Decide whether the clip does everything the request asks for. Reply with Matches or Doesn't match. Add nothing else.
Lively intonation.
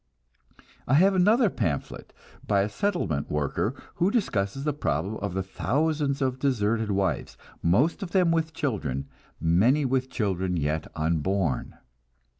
Matches